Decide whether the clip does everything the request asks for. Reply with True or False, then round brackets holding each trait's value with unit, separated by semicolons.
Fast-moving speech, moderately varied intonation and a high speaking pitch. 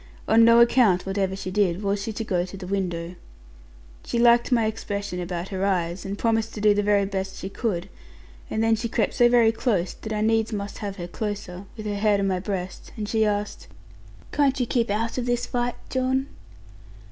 True (210 wpm; 3.0 semitones; 205 Hz)